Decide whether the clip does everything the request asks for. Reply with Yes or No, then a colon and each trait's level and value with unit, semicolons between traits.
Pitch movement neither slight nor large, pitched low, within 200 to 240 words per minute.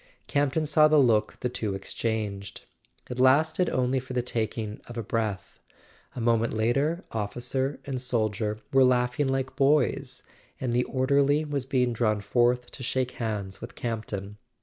No: average, 3.3 semitones; low, 125 Hz; average, 155 wpm